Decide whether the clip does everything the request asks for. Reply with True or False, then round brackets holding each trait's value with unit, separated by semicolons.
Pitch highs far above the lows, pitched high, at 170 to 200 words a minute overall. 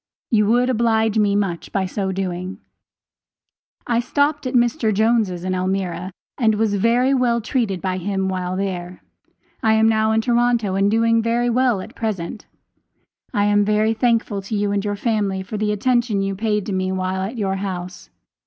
False (3.2 semitones; 210 Hz; 180 wpm)